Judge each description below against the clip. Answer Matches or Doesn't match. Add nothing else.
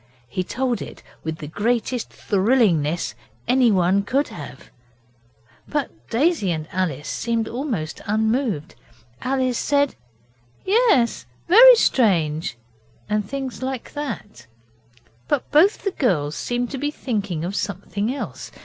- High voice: Matches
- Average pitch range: Doesn't match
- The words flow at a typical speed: Doesn't match